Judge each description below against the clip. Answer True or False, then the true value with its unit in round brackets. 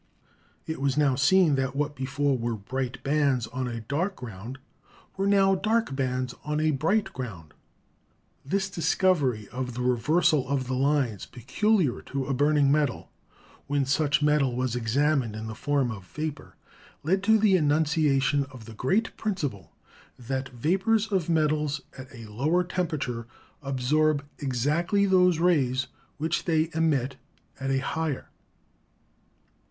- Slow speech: False (145 wpm)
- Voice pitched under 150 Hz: True (140 Hz)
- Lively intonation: False (4.1 semitones)